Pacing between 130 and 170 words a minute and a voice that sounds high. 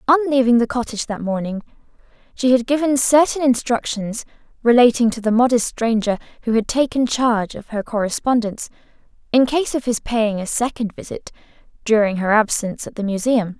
Yes: average, 160 wpm; high, 235 Hz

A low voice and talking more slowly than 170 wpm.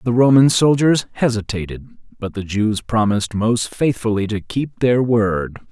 Yes: low, 115 Hz; average, 145 wpm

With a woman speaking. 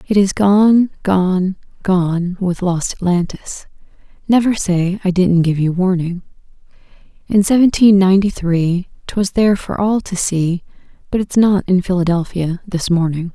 Yes: female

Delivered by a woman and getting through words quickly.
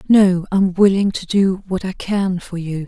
Yes: female; fast, 210 wpm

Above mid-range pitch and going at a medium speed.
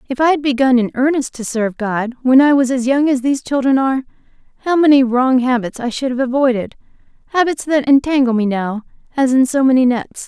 No: very high, 260 Hz; fast, 210 wpm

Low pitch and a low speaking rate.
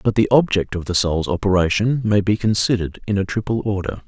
No: low, 100 Hz; fast, 205 wpm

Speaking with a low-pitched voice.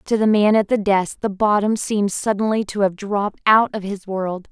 No: high, 205 Hz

